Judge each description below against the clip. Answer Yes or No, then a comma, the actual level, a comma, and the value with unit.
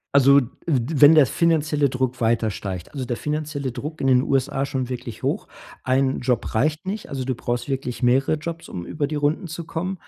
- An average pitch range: Yes, average, 3.6 semitones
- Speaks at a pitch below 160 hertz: Yes, low, 135 Hz